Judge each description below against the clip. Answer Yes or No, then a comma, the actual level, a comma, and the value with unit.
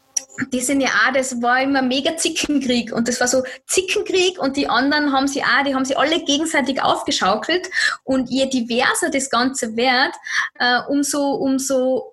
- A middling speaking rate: Yes, average, 175 wpm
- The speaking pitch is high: Yes, very high, 270 Hz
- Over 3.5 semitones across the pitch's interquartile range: No, average, 2.7 semitones